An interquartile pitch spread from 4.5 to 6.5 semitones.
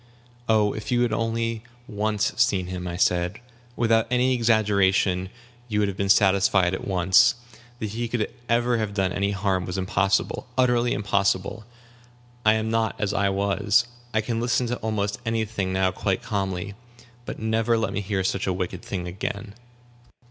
No: average, 2.9 semitones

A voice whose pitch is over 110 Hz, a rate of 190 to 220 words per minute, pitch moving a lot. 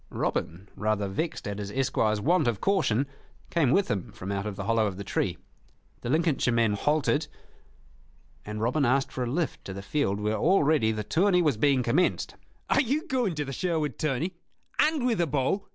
Yes: low, 135 Hz; average, 195 wpm; wide, 7.7 semitones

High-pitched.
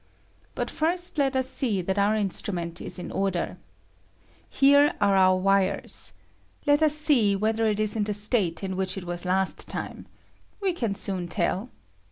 Yes: high, 200 Hz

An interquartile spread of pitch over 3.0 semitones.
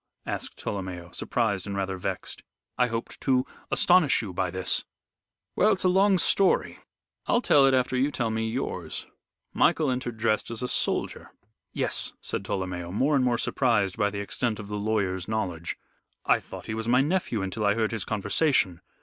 Yes: average, 4.7 semitones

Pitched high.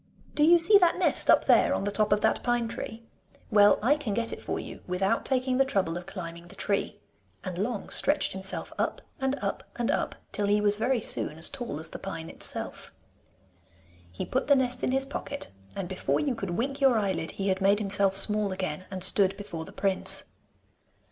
Yes: high, 205 Hz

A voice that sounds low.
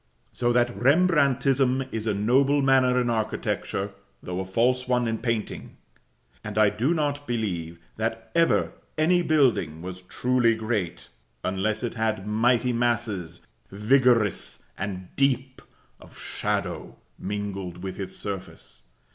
Yes: low, 115 Hz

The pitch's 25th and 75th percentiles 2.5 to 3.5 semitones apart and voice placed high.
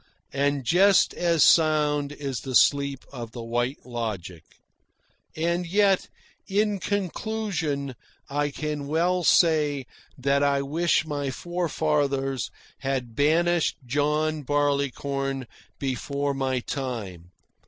No: average, 3.2 semitones; medium, 145 Hz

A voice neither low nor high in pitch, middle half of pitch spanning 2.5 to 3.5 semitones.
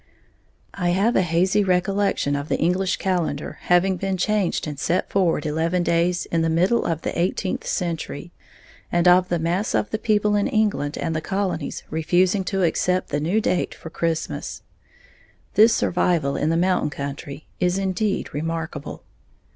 Yes: medium, 175 Hz; average, 2.9 semitones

